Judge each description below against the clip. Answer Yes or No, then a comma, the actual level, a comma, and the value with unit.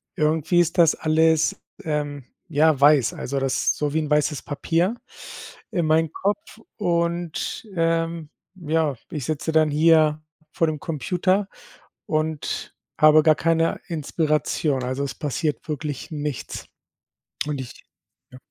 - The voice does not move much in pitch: Yes, narrow, 2.0 semitones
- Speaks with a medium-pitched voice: Yes, medium, 155 Hz